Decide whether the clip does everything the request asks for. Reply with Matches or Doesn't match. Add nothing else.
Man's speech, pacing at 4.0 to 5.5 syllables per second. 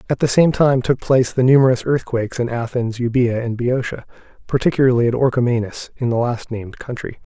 Doesn't match